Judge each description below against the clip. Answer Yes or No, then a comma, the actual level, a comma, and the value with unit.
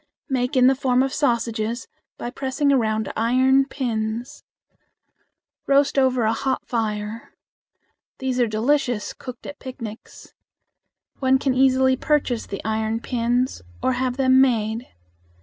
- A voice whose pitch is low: No, very high, 250 Hz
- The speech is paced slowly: Yes, slow, 130 wpm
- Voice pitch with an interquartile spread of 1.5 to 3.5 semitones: Yes, average, 2.7 semitones